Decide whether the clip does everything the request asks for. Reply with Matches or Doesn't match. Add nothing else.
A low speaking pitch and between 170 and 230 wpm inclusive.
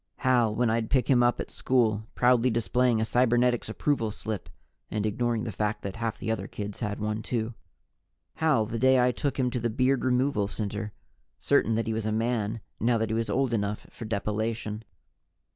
Matches